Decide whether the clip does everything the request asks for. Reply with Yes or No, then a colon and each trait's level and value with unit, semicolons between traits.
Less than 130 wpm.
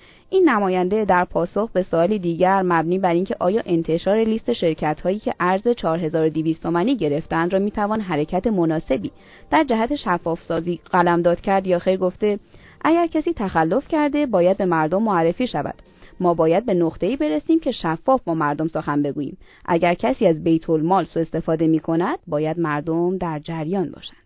No: fast, 165 wpm